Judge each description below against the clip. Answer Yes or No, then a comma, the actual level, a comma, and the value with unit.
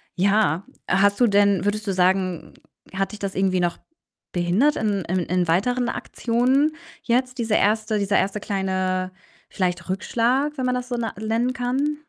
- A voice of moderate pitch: No, high, 205 Hz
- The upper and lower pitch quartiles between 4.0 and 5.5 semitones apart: Yes, average, 4.6 semitones